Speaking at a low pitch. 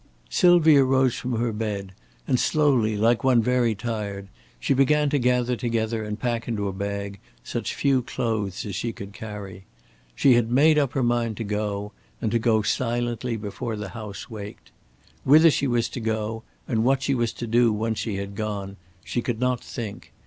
Yes: low, 115 Hz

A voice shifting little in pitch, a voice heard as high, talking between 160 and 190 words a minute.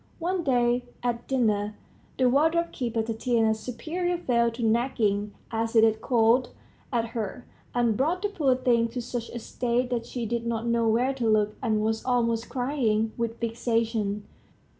Yes: narrow, 2.0 semitones; high, 235 Hz; average, 165 wpm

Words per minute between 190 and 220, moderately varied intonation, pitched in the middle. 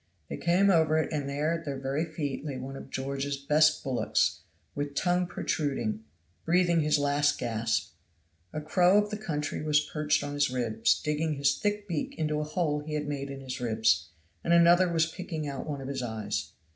Yes: average, 195 wpm; average, 3.1 semitones; medium, 150 Hz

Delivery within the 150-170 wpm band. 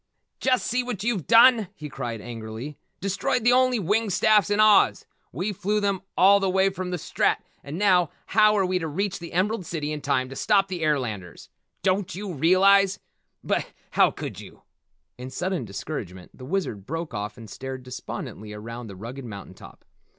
No: average, 185 wpm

